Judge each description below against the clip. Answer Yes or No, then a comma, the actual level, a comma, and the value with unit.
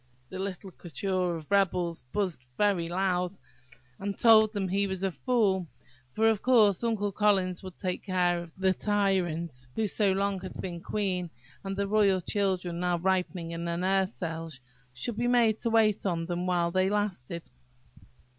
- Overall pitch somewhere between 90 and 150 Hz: No, high, 190 Hz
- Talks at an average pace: Yes, average, 170 wpm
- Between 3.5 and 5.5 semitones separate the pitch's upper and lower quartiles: No, narrow, 2.6 semitones